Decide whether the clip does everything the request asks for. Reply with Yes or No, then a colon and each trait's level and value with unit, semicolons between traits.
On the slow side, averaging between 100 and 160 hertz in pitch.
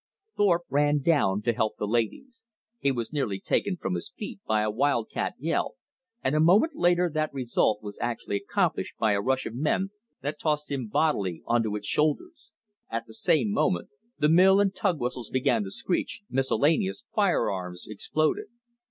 No: average, 180 wpm; low, 135 Hz